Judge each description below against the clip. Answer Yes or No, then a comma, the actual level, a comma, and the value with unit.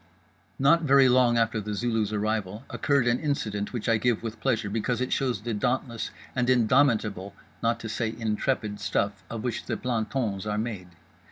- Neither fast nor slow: Yes, average, 170 wpm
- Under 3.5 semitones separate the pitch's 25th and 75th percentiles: Yes, average, 2.8 semitones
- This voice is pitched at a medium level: No, low, 115 Hz